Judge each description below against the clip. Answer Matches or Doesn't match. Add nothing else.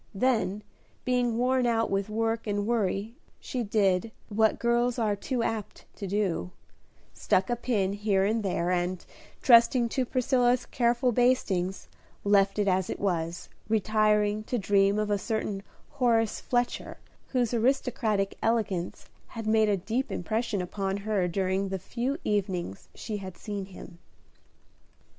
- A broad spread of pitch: Doesn't match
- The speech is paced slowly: Doesn't match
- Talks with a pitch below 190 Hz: Doesn't match